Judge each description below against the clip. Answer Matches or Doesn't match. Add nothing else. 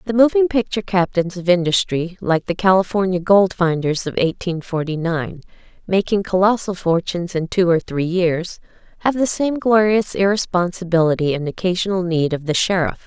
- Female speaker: Matches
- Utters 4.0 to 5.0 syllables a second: Doesn't match